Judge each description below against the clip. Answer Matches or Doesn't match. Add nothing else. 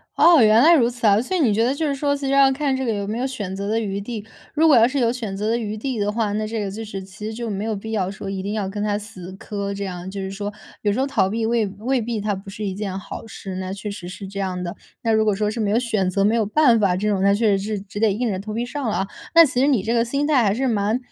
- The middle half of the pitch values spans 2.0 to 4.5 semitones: Matches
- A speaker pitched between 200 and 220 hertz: Matches